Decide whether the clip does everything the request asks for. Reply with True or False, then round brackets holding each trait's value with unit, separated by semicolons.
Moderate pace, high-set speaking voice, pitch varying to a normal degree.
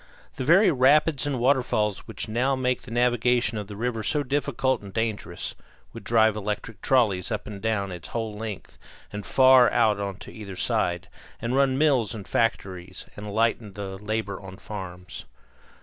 False (165 wpm; 110 Hz; 3.9 semitones)